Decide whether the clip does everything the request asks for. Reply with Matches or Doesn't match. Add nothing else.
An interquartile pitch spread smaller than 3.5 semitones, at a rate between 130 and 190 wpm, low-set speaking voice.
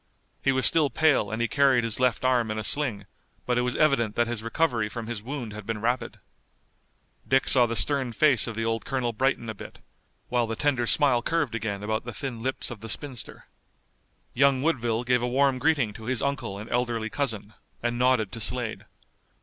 Doesn't match